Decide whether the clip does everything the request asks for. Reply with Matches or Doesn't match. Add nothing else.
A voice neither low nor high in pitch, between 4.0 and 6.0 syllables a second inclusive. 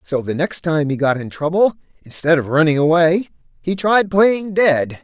Matches